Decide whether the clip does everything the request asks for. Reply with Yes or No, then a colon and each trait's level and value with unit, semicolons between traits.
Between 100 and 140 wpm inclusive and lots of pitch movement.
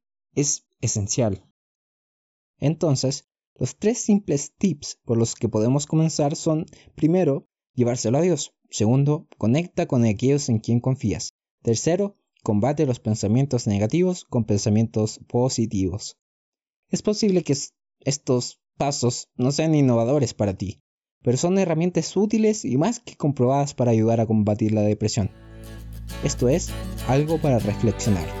Yes: average, 130 wpm; wide, 6.2 semitones